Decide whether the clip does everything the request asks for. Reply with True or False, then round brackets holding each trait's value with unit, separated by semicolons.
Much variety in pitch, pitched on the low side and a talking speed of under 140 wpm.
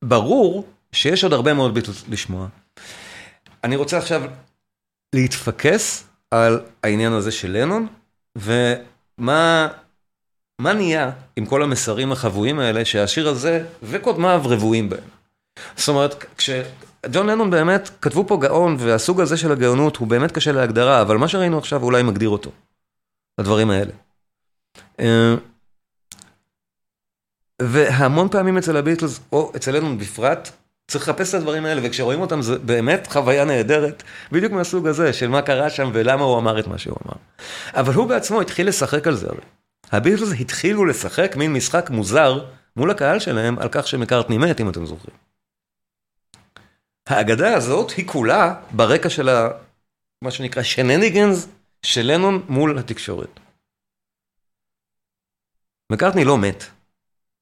True (5.8 semitones; 130 Hz; 130 wpm)